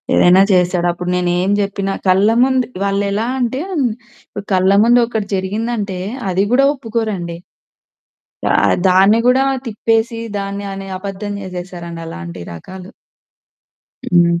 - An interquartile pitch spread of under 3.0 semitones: No, average, 3.6 semitones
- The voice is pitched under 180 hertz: No, high, 195 Hz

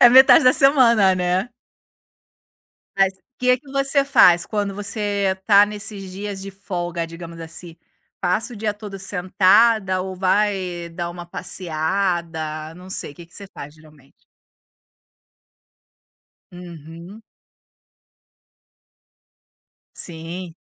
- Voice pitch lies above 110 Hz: Yes, high, 190 Hz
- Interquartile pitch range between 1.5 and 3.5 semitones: Yes, average, 3.2 semitones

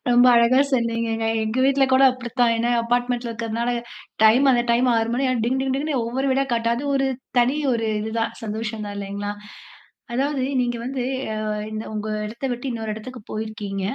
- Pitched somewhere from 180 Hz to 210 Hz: No, high, 235 Hz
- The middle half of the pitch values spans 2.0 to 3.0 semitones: Yes, narrow, 2.4 semitones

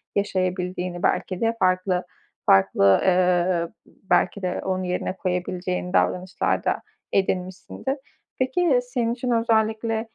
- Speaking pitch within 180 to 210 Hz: Yes, medium, 185 Hz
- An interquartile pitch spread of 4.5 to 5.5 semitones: No, average, 3.7 semitones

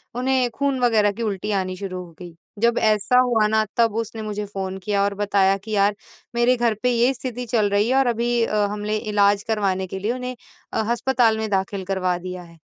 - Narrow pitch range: No, average, 3.2 semitones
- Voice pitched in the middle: No, high, 215 Hz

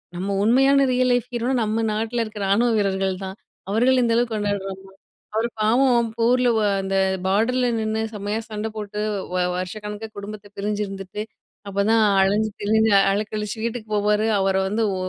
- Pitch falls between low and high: No, high, 215 Hz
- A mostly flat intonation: Yes, narrow, 2.3 semitones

